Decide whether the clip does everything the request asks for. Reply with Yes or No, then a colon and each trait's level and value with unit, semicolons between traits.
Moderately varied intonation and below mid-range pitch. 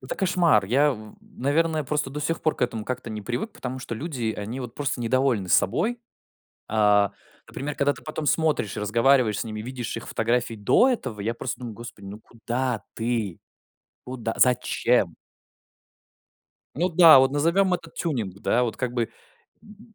Yes: average, 4.9 semitones; low, 125 Hz